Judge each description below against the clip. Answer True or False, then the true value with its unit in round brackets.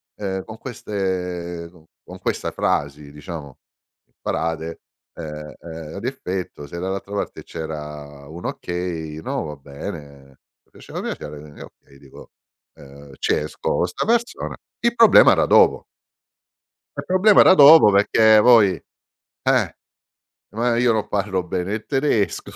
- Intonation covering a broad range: True (6.0 semitones)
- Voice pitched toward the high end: False (90 Hz)